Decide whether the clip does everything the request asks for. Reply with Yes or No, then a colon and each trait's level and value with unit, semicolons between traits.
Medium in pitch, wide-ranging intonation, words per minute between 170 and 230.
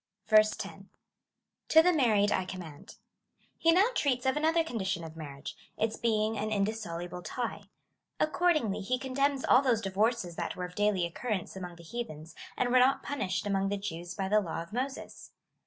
No: high, 215 Hz; wide, 5.7 semitones; average, 180 wpm